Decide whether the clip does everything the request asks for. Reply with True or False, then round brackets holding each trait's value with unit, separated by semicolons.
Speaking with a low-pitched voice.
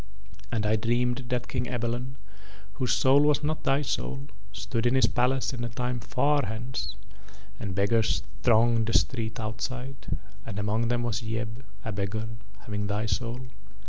True (115 Hz)